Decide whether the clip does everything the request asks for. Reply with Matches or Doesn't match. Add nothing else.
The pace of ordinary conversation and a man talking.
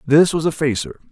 Doesn't match